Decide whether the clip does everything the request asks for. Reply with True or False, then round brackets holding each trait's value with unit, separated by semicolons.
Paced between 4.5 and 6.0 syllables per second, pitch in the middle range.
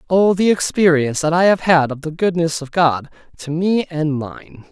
True (4.7 syllables/s; 165 Hz)